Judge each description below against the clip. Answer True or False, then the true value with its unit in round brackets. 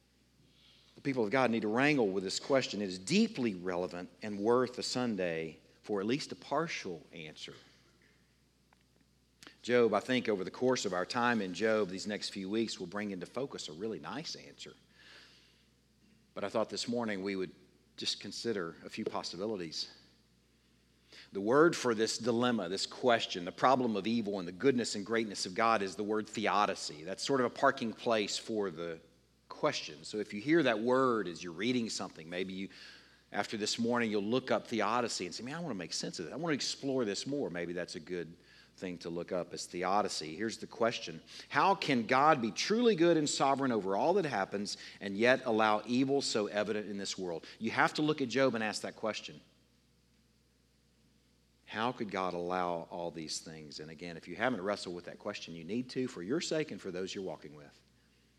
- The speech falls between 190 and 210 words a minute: True (200 wpm)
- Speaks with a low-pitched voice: True (105 Hz)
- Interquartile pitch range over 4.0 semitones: True (5.5 semitones)